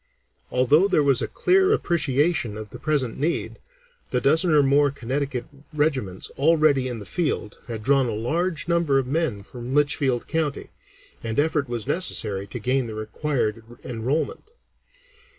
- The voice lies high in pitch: No, low, 135 Hz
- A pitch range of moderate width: Yes, average, 4.6 semitones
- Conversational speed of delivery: Yes, average, 150 wpm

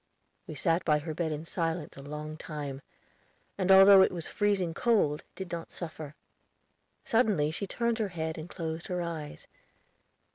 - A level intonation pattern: No, average, 3.8 semitones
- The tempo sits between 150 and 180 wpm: Yes, average, 160 wpm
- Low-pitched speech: No, medium, 165 Hz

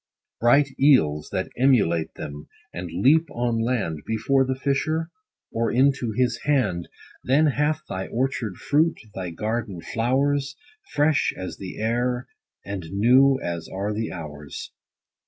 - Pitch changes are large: Yes, wide, 6.6 semitones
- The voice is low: Yes, low, 120 Hz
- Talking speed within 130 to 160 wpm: Yes, slow, 135 wpm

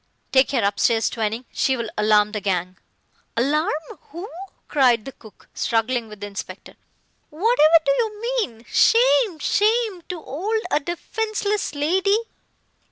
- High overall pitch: Yes, very high, 290 Hz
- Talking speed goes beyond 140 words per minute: No, slow, 135 wpm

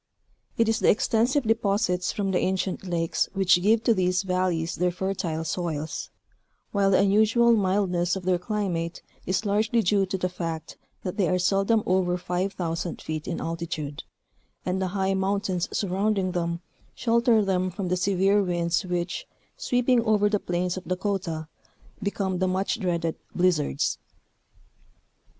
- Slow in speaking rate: No, average, 150 wpm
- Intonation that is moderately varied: No, narrow, 2.3 semitones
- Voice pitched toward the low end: No, medium, 185 Hz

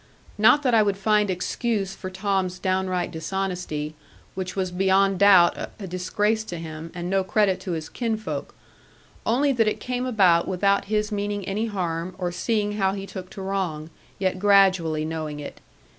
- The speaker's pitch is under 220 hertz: Yes, high, 190 Hz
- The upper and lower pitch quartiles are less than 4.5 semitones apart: Yes, narrow, 2.5 semitones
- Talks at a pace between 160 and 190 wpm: Yes, average, 170 wpm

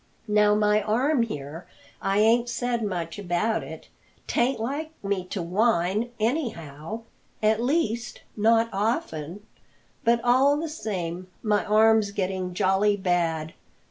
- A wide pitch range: No, average, 4.0 semitones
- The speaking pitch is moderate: No, high, 210 Hz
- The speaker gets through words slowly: Yes, slow, 125 wpm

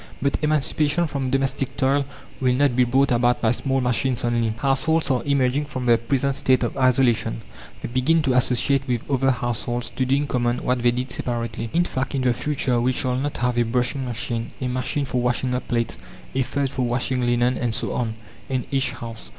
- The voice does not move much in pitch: Yes, narrow, 2.0 semitones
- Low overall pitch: Yes, low, 125 Hz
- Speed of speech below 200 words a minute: No, fast, 205 wpm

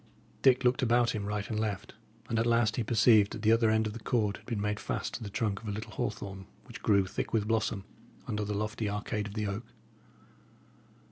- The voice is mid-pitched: No, low, 110 Hz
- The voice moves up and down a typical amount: No, narrow, 1.8 semitones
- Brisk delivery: Yes, fast, 225 wpm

